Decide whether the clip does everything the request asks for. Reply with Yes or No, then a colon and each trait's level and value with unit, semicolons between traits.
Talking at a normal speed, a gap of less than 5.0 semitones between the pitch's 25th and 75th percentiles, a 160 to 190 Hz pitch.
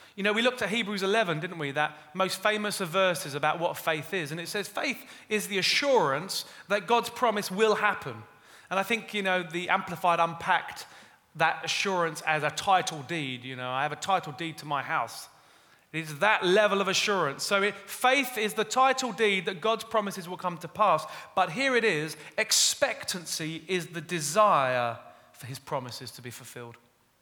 No: average, 190 wpm; average, 5.3 semitones; medium, 185 Hz